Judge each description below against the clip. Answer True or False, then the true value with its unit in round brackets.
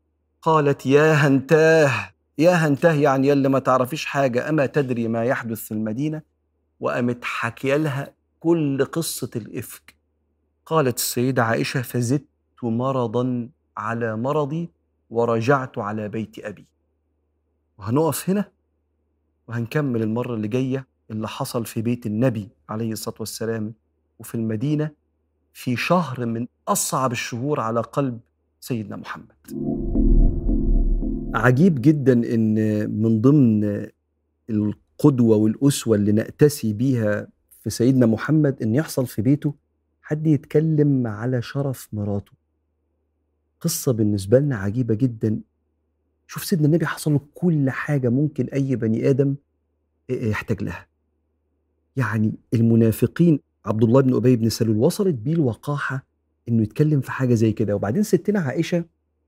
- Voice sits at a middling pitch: False (120 Hz)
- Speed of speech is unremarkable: True (120 wpm)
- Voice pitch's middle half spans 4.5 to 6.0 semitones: True (5.1 semitones)